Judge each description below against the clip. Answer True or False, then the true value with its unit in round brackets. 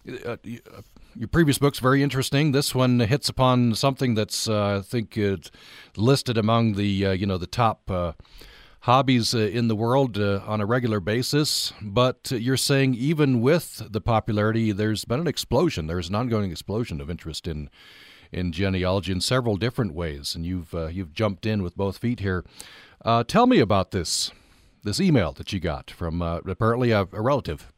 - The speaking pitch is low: True (110 Hz)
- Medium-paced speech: True (185 wpm)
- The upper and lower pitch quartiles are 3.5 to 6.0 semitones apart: True (4.6 semitones)